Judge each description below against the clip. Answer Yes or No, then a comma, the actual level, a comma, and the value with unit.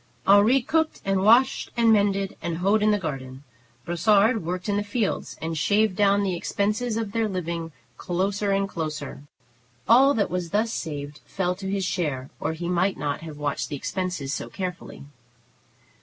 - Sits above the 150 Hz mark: Yes, high, 190 Hz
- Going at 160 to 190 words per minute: Yes, average, 170 wpm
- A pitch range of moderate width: Yes, average, 4.0 semitones